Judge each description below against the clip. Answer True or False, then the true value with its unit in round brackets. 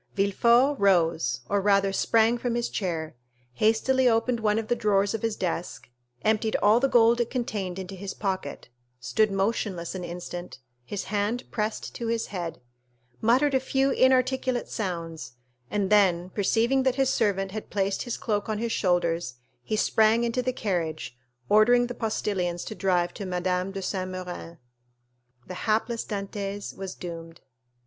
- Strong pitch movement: False (4.1 semitones)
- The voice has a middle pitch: False (205 Hz)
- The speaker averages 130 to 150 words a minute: False (160 wpm)